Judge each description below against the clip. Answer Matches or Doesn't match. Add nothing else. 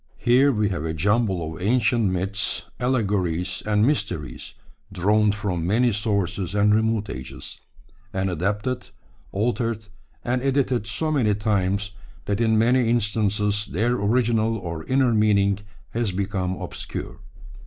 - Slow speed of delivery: Matches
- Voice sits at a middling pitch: Doesn't match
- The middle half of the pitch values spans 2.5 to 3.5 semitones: Matches